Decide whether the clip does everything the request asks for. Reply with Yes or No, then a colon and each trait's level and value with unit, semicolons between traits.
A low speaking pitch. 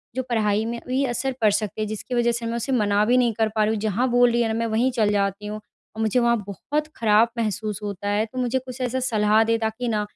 No: high, 225 Hz